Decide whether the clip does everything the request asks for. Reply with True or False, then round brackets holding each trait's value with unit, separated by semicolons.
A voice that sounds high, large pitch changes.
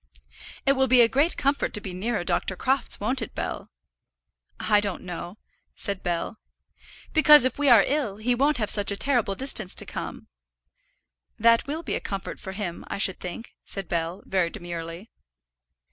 True (210 Hz; 5.7 semitones)